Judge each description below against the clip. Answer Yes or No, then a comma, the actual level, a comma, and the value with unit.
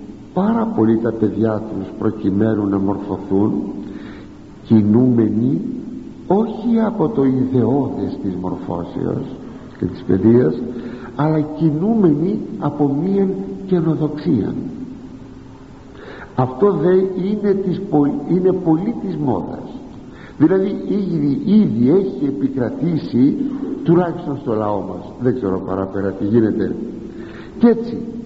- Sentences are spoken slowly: Yes, slow, 100 wpm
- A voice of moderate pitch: Yes, medium, 145 Hz